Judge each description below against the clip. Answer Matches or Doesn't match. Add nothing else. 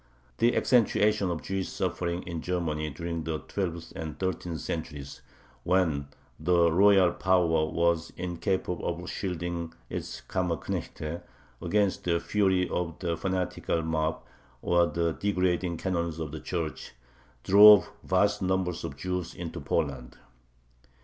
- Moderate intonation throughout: Doesn't match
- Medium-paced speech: Doesn't match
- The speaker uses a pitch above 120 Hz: Doesn't match